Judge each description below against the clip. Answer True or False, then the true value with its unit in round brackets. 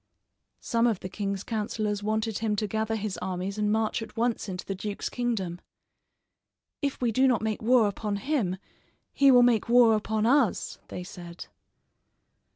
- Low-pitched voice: False (215 Hz)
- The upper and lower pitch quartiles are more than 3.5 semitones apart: False (2.7 semitones)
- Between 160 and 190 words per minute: True (165 wpm)